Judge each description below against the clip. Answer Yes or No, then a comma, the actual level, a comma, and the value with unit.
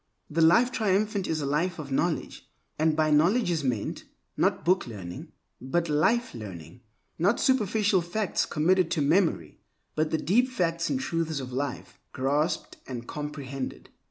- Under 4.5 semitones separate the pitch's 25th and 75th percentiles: No, average, 4.9 semitones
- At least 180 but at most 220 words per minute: No, average, 150 wpm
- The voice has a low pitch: No, medium, 160 Hz